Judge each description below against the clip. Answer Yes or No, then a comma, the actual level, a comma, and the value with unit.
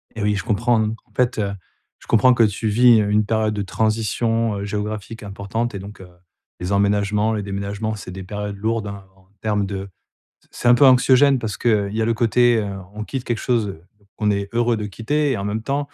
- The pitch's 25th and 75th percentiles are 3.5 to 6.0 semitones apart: No, narrow, 2.4 semitones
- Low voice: Yes, low, 110 Hz